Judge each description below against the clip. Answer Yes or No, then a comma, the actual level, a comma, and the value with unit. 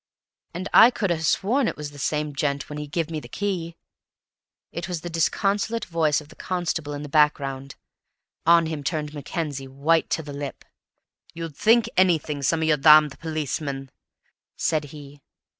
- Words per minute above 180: No, average, 175 wpm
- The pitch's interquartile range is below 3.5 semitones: Yes, narrow, 2.6 semitones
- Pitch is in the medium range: Yes, medium, 155 Hz